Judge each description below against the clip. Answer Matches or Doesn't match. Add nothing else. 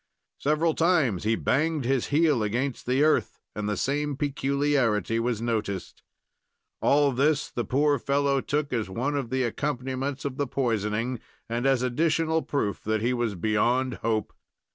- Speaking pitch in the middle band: Doesn't match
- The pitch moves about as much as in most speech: Matches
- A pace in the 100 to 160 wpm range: Matches